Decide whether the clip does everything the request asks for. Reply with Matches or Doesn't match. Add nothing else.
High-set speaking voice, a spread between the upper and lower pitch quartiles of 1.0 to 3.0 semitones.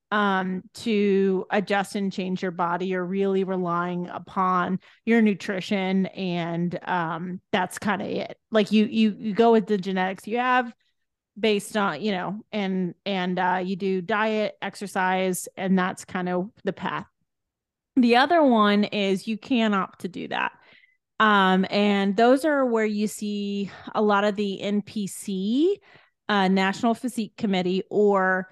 Matches